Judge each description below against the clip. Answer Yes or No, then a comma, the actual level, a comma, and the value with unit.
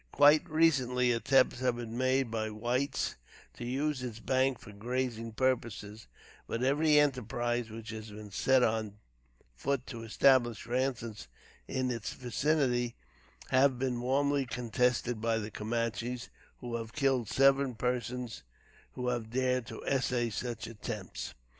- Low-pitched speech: Yes, low, 125 Hz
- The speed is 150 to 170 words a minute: No, slow, 135 wpm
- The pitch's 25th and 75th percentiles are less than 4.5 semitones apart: Yes, narrow, 2.4 semitones